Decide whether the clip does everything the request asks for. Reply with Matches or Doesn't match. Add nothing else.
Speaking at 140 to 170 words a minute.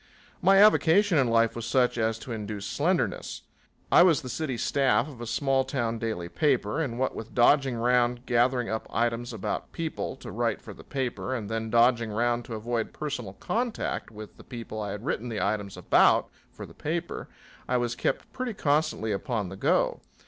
Doesn't match